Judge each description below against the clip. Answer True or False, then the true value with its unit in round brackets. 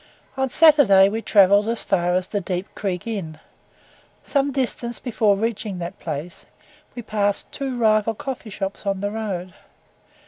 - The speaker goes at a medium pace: True (150 wpm)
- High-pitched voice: True (205 Hz)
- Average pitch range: True (3.5 semitones)